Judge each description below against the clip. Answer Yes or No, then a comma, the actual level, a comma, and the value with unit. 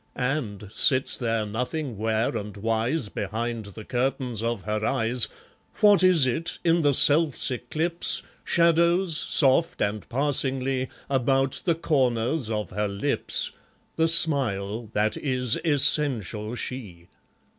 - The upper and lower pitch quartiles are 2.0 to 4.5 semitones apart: No, average, 5.3 semitones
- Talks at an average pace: No, slow, 125 wpm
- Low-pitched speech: Yes, low, 125 Hz